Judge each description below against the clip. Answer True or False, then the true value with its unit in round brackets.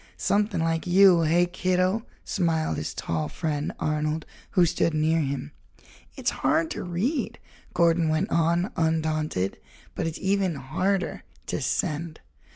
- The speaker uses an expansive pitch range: False (2.8 semitones)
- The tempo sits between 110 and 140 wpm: True (135 wpm)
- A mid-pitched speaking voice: True (165 Hz)